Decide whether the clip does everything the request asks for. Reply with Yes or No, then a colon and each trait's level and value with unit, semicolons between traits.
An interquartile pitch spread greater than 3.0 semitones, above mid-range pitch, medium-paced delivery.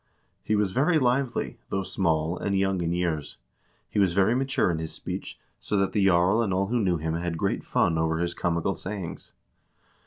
No: average, 3.5 semitones; very low, 95 Hz; average, 195 wpm